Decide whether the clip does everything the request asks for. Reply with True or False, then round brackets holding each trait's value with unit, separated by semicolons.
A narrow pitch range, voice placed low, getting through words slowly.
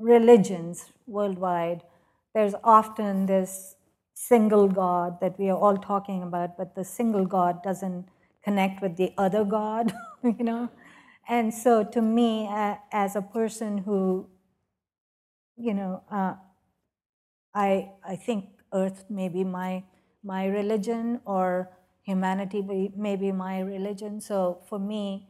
False (2.3 semitones; 195 Hz; 130 wpm)